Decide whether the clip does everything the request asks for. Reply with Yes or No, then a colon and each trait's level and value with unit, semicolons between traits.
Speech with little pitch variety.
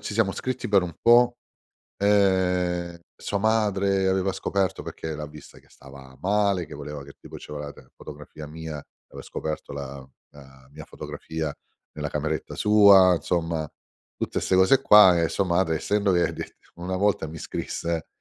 No: average, 4.4 semitones